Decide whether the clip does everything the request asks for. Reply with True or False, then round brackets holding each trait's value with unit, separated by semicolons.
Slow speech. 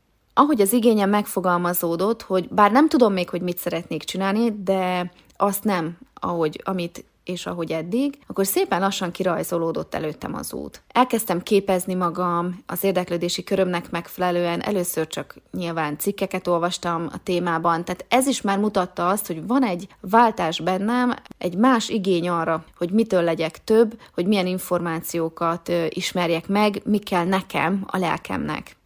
False (150 wpm)